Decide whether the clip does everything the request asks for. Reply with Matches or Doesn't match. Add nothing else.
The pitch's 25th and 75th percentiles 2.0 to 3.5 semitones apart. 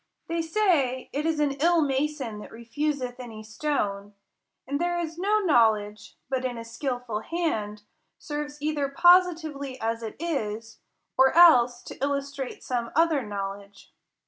Doesn't match